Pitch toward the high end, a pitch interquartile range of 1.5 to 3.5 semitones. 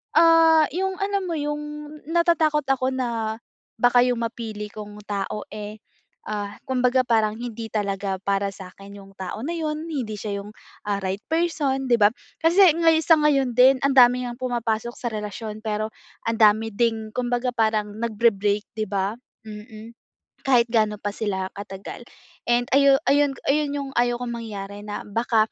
No: high, 235 Hz; average, 4.5 semitones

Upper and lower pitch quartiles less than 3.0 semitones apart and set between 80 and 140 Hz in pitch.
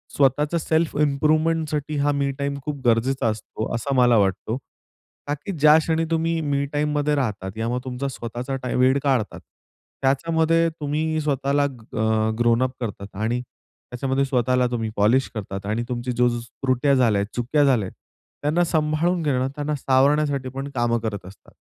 No: average, 3.8 semitones; low, 135 Hz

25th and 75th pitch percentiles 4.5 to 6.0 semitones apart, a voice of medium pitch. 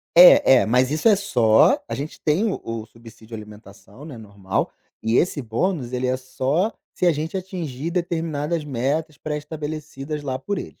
Yes: wide, 5.4 semitones; medium, 145 Hz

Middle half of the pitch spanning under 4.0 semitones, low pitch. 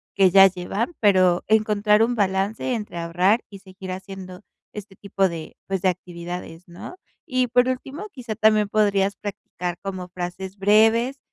No: average, 2.8 semitones; high, 195 Hz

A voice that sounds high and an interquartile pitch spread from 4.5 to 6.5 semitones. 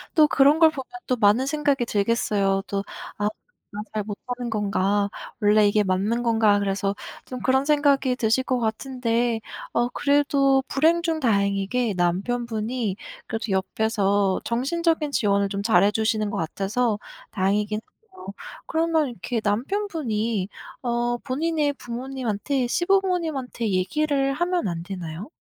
Yes: high, 235 Hz; average, 5.1 semitones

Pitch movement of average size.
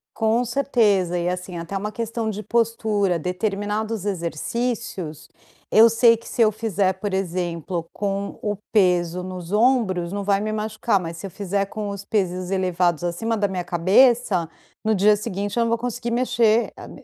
Yes: average, 3.6 semitones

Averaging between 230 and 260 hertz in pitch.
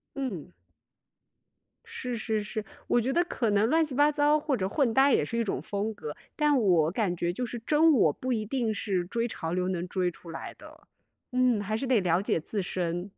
No: high, 220 Hz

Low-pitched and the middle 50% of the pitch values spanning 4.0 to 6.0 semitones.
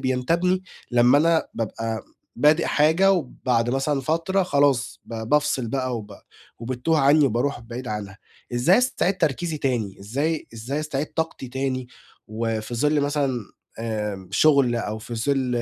Yes: low, 130 Hz; average, 4.5 semitones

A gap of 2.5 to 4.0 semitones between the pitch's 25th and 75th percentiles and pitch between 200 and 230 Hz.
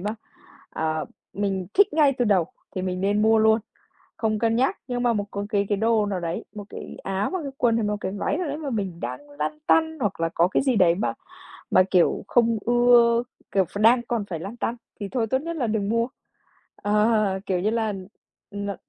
Yes: average, 3.5 semitones; high, 215 Hz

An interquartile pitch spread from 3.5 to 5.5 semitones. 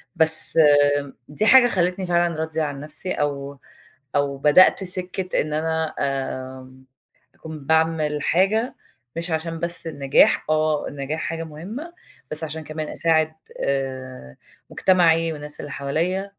No: average, 2.9 semitones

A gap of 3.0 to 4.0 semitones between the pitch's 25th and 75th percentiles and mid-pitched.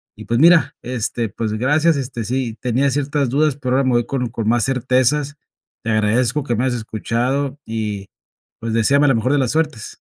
No: average, 3.5 semitones; low, 125 Hz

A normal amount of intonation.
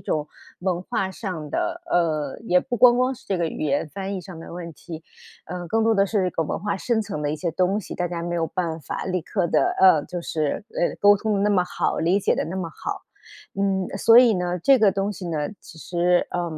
Yes: average, 3.2 semitones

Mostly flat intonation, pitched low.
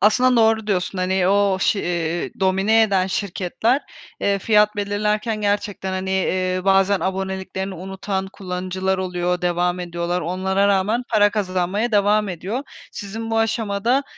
No: narrow, 2.3 semitones; high, 195 Hz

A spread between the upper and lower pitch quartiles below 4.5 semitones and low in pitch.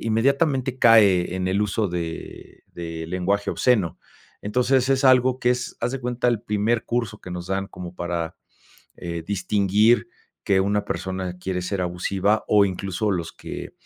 No: average, 4.8 semitones; low, 100 Hz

